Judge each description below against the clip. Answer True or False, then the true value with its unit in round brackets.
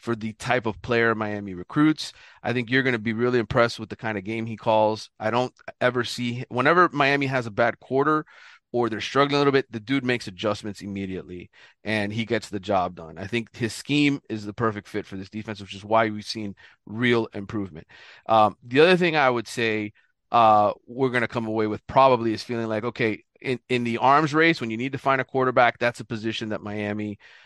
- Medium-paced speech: False (225 wpm)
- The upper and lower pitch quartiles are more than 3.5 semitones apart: False (3.0 semitones)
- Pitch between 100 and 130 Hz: True (115 Hz)